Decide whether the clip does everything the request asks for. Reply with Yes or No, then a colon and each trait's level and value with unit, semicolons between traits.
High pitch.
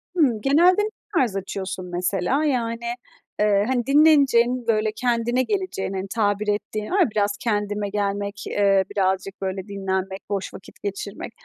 Yes: high, 210 Hz